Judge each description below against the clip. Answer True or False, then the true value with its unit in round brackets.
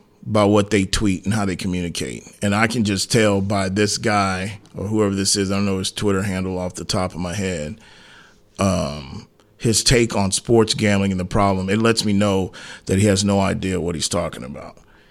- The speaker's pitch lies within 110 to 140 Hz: False (100 Hz)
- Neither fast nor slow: False (215 wpm)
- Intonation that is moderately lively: False (2.0 semitones)